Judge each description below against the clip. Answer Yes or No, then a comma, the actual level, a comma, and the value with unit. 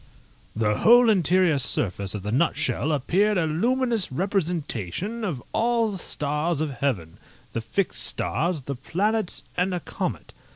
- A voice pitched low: No, medium, 170 Hz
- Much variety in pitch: Yes, wide, 6.9 semitones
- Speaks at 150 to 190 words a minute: No, average, 140 wpm